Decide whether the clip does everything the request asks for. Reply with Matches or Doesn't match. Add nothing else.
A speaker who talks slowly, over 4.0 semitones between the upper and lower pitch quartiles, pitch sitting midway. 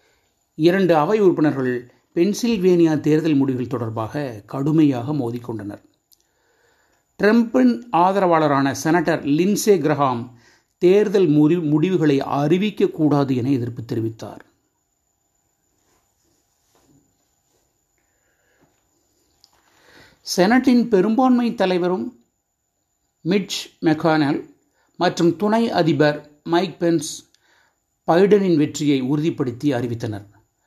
Matches